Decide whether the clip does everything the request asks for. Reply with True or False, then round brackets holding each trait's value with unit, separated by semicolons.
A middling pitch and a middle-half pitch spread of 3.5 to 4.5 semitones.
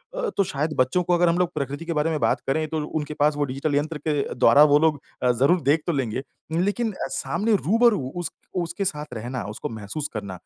True (150 Hz; 4.2 semitones)